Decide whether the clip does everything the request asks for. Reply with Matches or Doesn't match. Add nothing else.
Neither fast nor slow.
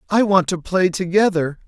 Matches